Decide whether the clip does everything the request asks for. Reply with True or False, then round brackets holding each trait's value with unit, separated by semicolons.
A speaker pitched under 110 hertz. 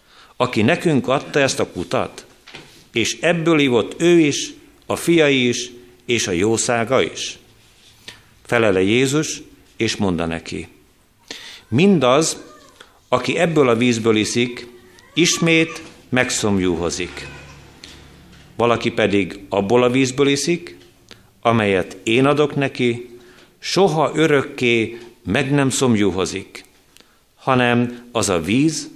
False (120 Hz)